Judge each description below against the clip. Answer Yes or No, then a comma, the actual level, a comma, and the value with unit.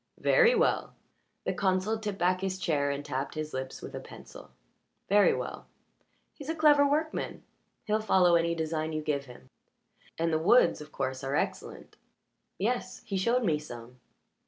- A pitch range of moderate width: No, wide, 6.4 semitones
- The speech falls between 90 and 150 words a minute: No, average, 165 wpm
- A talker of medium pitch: Yes, medium, 175 Hz